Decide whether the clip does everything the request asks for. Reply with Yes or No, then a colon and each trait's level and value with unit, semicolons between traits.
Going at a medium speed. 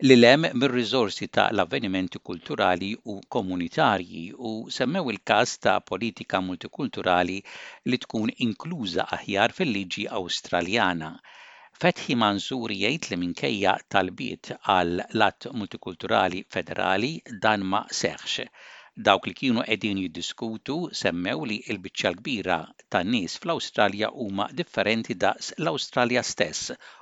No: slow, 120 wpm